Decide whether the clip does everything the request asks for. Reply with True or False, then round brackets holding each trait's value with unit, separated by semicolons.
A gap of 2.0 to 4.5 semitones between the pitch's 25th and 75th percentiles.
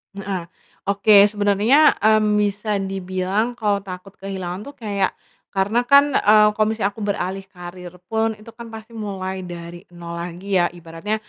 True (2.6 semitones)